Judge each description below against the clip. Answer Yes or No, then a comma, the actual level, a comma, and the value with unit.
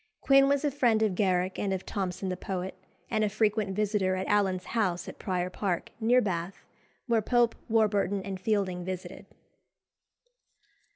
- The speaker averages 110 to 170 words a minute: Yes, average, 160 wpm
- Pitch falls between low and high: No, high, 200 Hz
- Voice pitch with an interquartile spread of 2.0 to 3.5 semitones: Yes, average, 2.8 semitones